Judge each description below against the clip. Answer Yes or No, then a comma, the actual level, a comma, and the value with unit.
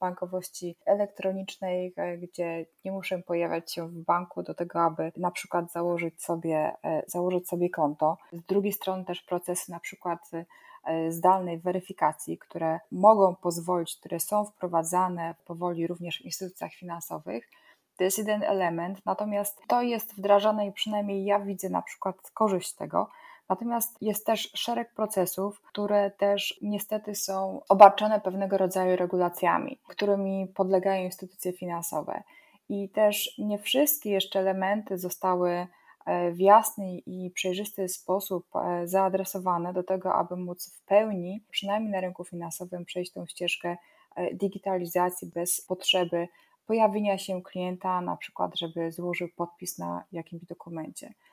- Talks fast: No, average, 130 wpm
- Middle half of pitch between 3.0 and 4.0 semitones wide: No, narrow, 2.4 semitones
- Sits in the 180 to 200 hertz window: Yes, medium, 185 Hz